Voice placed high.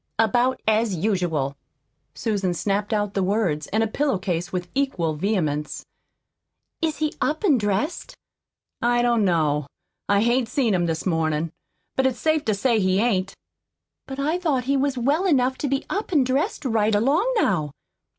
Yes: high, 220 Hz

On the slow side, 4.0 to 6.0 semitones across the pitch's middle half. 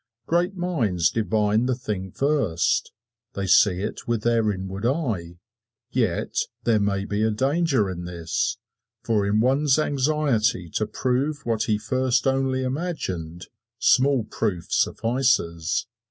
Yes: slow, 125 wpm; average, 5.3 semitones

